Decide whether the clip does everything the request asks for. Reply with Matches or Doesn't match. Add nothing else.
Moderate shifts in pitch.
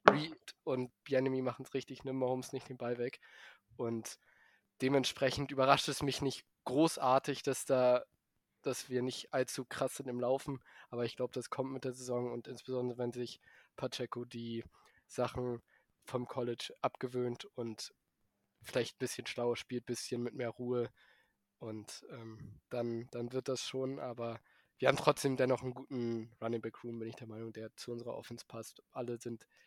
Doesn't match